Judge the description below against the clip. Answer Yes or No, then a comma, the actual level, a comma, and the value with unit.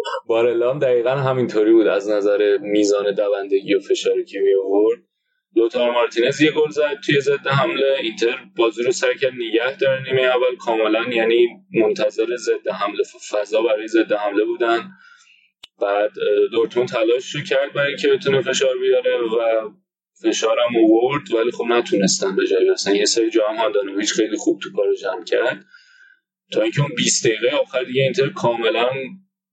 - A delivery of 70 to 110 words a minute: No, fast, 155 wpm